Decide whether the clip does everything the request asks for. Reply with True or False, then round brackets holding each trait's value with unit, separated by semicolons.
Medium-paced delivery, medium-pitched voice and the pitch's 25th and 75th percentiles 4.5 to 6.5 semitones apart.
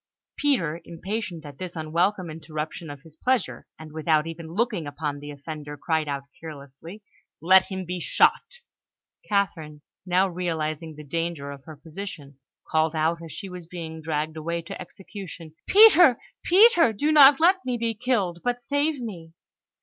True (155 wpm; 170 Hz; 4.8 semitones)